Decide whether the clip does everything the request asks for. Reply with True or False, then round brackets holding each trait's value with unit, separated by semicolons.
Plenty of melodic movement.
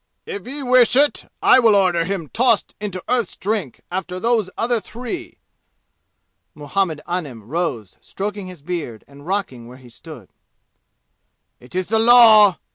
True (5.7 semitones)